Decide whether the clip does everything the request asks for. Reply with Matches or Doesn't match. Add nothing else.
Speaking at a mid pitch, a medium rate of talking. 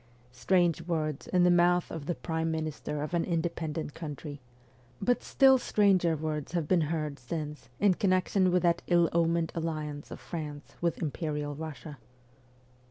Matches